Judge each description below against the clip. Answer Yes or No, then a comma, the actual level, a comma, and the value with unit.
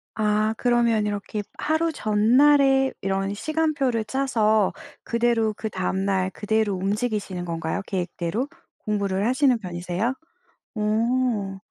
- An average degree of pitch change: Yes, average, 4.0 semitones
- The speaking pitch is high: Yes, high, 215 Hz